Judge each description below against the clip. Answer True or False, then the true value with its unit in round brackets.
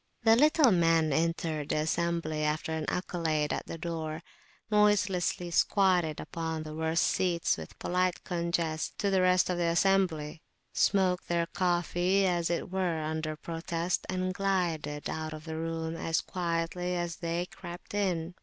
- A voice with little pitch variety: True (2.2 semitones)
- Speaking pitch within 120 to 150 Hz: False (170 Hz)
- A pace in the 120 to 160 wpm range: True (155 wpm)